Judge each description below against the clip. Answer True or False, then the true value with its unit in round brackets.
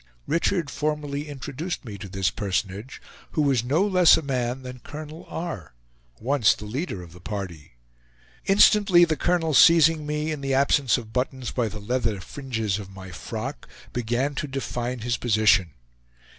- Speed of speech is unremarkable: True (160 wpm)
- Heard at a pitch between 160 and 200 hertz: False (130 Hz)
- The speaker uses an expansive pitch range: True (5.9 semitones)